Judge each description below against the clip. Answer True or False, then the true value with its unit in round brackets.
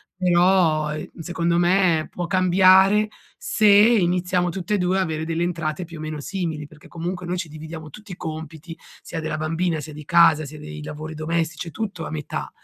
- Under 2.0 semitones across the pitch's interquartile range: False (2.7 semitones)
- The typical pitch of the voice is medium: True (170 Hz)